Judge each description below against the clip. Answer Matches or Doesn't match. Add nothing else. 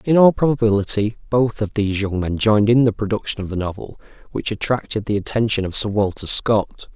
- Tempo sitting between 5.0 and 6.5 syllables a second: Matches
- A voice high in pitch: Doesn't match